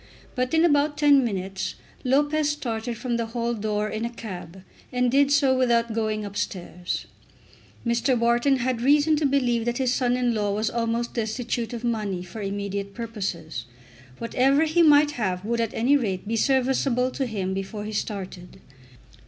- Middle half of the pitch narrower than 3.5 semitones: No, average, 3.9 semitones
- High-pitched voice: Yes, high, 235 Hz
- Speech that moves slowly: No, average, 170 wpm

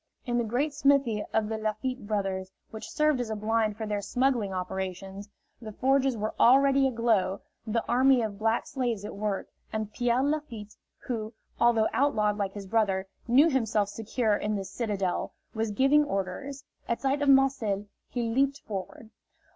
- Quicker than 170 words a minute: No, average, 165 wpm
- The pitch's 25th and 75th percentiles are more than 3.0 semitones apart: Yes, average, 4.2 semitones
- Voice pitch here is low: No, high, 225 Hz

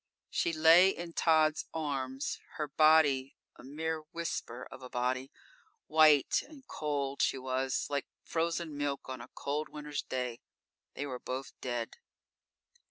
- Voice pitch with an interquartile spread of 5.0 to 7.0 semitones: No, average, 3.3 semitones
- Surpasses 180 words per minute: No, average, 140 wpm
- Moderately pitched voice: Yes, medium, 145 Hz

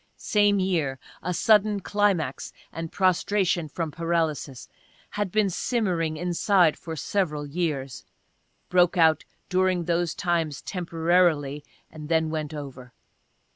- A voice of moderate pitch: Yes, medium, 170 Hz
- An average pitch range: Yes, average, 3.2 semitones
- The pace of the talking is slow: Yes, slow, 115 wpm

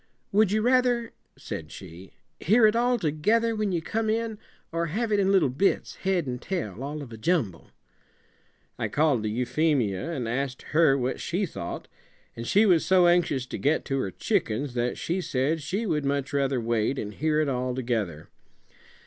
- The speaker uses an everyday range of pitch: No, wide, 7.6 semitones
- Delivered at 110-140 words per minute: No, average, 185 wpm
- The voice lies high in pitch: No, medium, 150 Hz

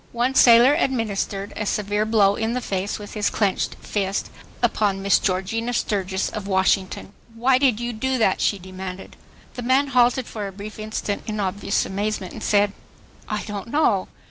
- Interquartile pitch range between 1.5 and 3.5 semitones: Yes, average, 3.2 semitones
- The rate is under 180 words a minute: Yes, average, 170 wpm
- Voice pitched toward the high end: Yes, high, 210 Hz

